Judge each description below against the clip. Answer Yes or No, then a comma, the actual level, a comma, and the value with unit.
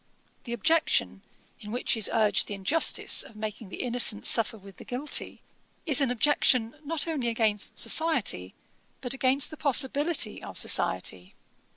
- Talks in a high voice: Yes, high, 240 Hz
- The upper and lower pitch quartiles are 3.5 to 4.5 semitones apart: No, average, 5.1 semitones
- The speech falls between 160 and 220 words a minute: No, average, 150 wpm